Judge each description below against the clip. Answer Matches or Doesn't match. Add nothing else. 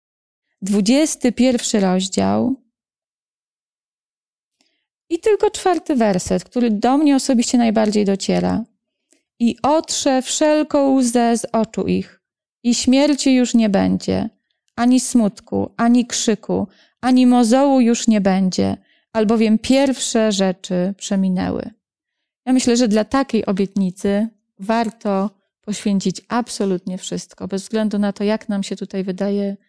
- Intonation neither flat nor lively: Matches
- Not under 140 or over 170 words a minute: Doesn't match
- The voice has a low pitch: Doesn't match